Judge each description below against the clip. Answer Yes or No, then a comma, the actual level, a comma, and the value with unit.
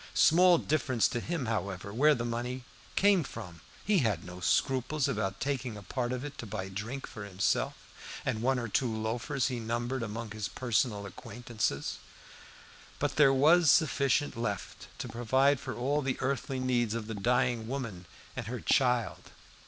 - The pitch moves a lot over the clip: No, average, 3.8 semitones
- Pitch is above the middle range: No, low, 120 Hz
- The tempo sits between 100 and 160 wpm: No, average, 170 wpm